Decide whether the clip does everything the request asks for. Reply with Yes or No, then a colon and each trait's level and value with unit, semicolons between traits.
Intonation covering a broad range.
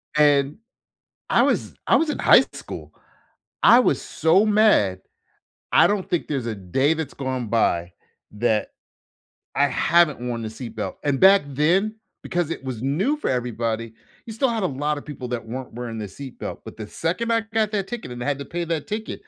Yes: wide, 7.9 semitones